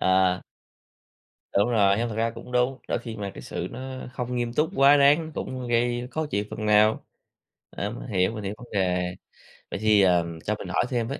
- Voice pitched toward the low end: Yes, low, 115 Hz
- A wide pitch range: No, average, 3.6 semitones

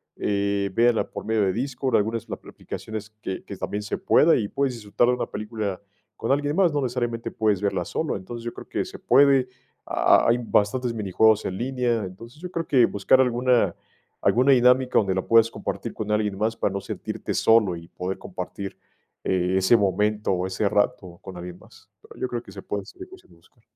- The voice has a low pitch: Yes, low, 110 Hz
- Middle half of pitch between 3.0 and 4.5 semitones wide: Yes, average, 3.9 semitones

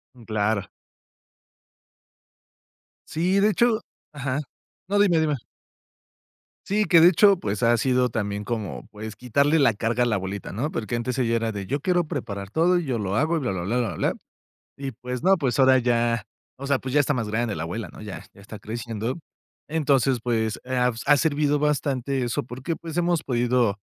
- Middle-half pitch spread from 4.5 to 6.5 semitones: Yes, average, 5.0 semitones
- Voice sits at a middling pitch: No, low, 125 Hz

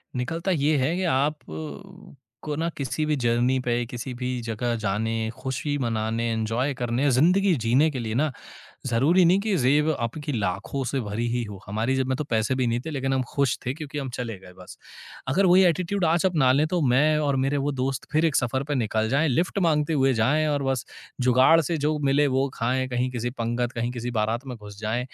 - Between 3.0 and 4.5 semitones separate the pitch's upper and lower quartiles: Yes, average, 4.2 semitones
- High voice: No, low, 130 Hz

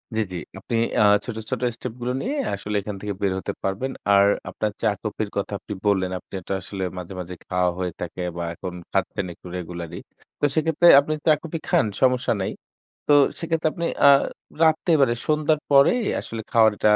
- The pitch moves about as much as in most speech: No, wide, 7.5 semitones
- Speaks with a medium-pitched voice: No, low, 105 Hz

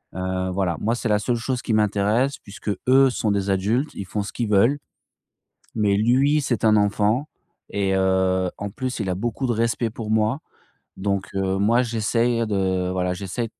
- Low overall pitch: Yes, low, 105 Hz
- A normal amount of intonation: Yes, average, 3.5 semitones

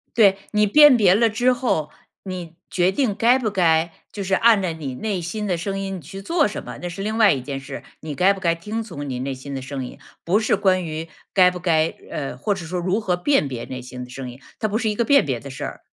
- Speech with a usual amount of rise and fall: No, wide, 5.8 semitones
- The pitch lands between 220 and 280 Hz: No, medium, 185 Hz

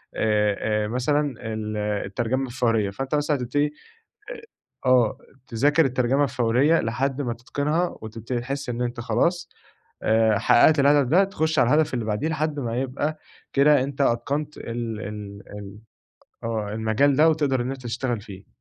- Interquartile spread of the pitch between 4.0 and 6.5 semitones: Yes, average, 4.5 semitones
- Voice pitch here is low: Yes, low, 125 Hz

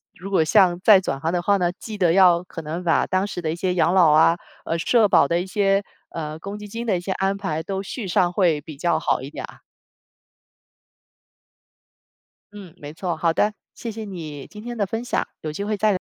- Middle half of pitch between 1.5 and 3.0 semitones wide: No, average, 3.5 semitones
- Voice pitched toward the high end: No, medium, 180 Hz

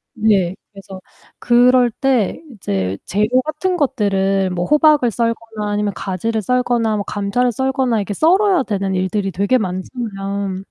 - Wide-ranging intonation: No, average, 4.4 semitones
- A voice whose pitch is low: No, high, 215 Hz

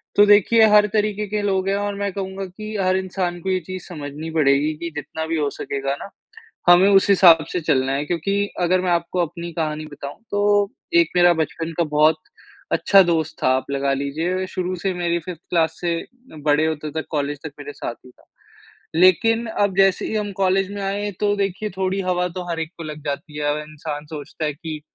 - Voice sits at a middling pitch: Yes, medium, 175 Hz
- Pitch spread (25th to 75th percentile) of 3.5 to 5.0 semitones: Yes, average, 4.1 semitones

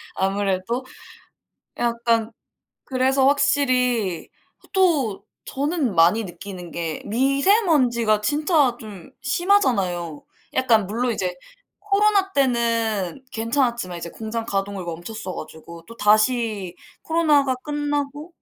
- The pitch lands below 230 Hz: No, high, 235 Hz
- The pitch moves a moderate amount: No, wide, 6.1 semitones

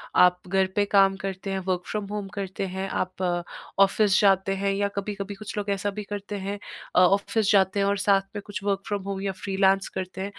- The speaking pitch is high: Yes, high, 195 Hz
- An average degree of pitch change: No, narrow, 1.0 semitones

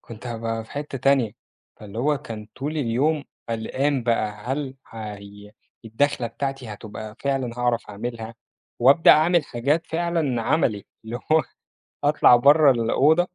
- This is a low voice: Yes, low, 125 Hz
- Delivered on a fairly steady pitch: No, average, 4.2 semitones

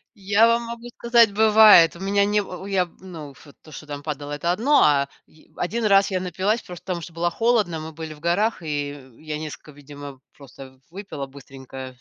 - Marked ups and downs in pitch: Yes, wide, 5.7 semitones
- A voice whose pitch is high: No, medium, 170 Hz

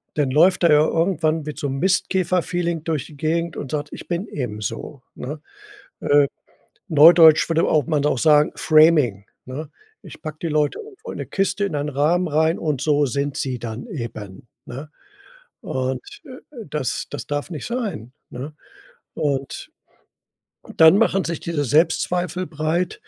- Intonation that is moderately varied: Yes, average, 3.3 semitones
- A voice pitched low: No, medium, 155 Hz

